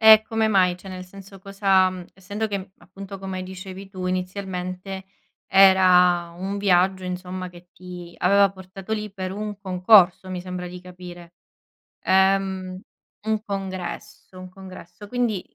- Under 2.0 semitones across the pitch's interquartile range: Yes, narrow, 1.3 semitones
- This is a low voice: No, high, 190 Hz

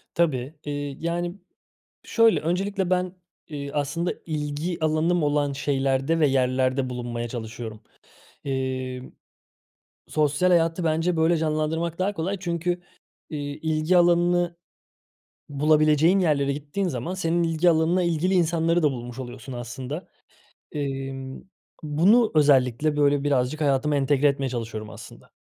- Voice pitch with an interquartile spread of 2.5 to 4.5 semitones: Yes, average, 4.1 semitones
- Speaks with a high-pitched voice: No, medium, 150 Hz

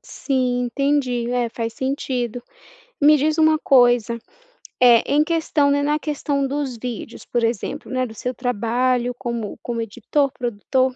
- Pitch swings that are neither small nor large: Yes, average, 3.0 semitones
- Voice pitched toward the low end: No, very high, 250 Hz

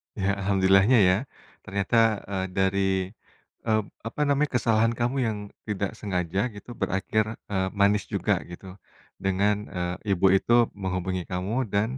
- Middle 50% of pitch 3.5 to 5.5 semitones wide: No, narrow, 2.5 semitones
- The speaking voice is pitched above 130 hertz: No, low, 100 Hz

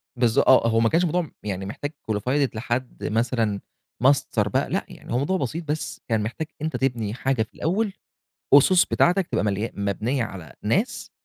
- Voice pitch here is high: No, low, 125 Hz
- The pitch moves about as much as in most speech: No, wide, 5.7 semitones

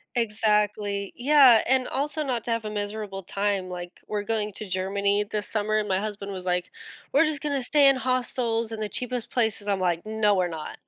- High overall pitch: Yes, high, 210 Hz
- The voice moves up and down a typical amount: Yes, average, 3.3 semitones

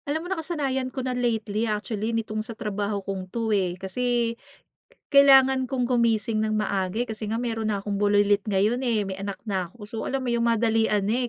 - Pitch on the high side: Yes, high, 225 Hz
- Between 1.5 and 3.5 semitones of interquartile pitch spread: Yes, average, 3.1 semitones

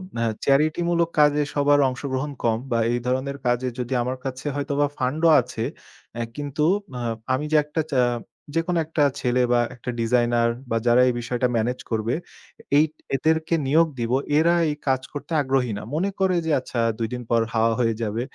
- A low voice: Yes, low, 130 Hz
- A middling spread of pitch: Yes, average, 3.7 semitones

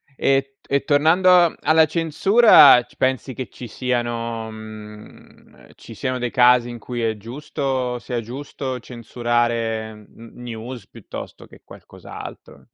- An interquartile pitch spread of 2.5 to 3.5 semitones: Yes, average, 2.9 semitones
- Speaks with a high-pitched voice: No, low, 125 Hz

